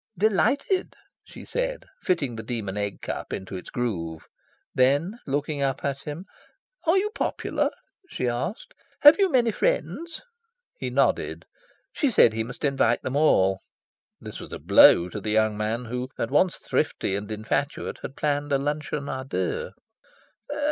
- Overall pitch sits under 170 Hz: Yes, medium, 140 Hz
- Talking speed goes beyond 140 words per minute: Yes, average, 155 wpm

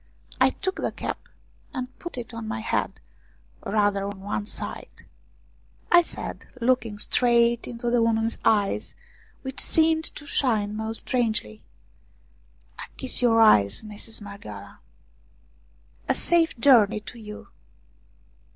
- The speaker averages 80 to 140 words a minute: Yes, slow, 135 wpm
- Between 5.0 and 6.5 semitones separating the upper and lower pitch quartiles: No, average, 3.2 semitones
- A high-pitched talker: Yes, high, 225 Hz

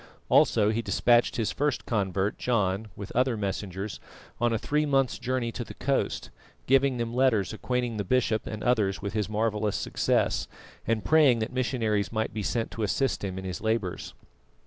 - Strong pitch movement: No, average, 3.3 semitones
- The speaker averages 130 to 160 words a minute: No, average, 175 wpm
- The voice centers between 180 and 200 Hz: No, low, 110 Hz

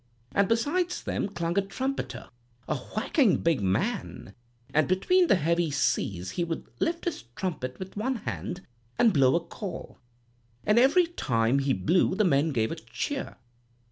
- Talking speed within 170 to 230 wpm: No, average, 160 wpm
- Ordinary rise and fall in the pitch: No, wide, 8.5 semitones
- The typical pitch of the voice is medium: Yes, medium, 180 Hz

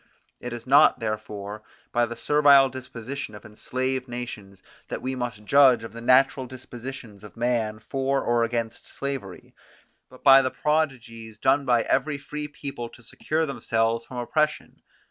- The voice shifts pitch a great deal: No, average, 3.1 semitones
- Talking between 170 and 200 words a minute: No, average, 155 wpm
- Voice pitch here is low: Yes, low, 125 Hz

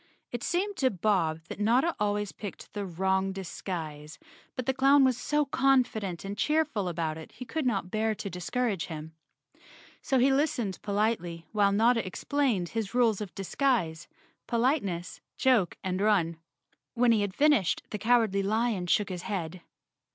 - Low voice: No, high, 210 Hz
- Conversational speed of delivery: Yes, average, 160 wpm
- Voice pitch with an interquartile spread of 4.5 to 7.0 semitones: Yes, average, 5.3 semitones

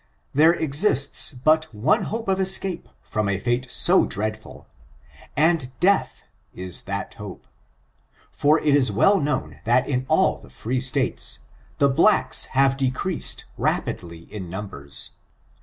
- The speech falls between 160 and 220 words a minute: No, slow, 135 wpm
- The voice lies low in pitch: Yes, low, 130 Hz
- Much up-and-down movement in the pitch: Yes, wide, 6.8 semitones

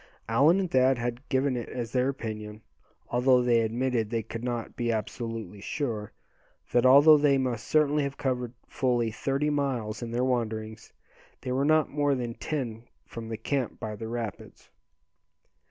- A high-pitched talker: No, low, 120 Hz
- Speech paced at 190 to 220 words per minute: No, average, 165 wpm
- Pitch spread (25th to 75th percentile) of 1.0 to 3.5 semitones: Yes, average, 3.1 semitones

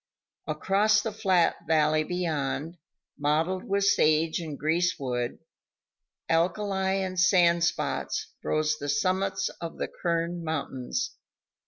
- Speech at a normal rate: No, slow, 110 wpm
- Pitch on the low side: No, medium, 170 Hz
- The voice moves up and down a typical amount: Yes, average, 3.5 semitones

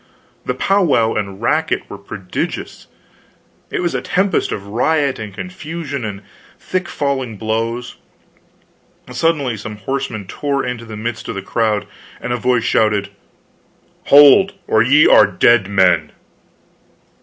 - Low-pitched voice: Yes, low, 120 Hz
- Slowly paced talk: Yes, slow, 130 wpm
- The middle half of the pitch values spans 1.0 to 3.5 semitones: No, average, 5.1 semitones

